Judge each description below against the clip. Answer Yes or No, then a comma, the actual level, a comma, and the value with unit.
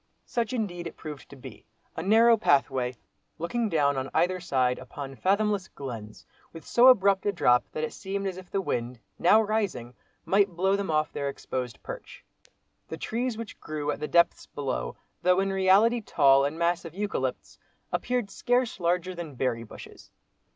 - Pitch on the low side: No, medium, 175 Hz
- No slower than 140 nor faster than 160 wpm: No, average, 170 wpm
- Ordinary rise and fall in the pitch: No, wide, 6.3 semitones